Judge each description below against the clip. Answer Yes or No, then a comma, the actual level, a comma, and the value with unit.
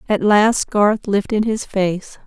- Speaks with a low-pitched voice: No, high, 205 Hz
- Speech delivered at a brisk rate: No, average, 160 wpm